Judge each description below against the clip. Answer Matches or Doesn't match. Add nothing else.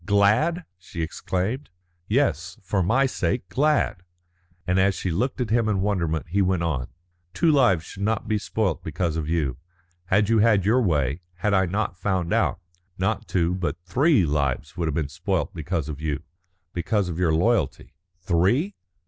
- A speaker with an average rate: Matches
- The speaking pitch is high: Doesn't match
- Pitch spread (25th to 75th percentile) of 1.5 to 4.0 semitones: Doesn't match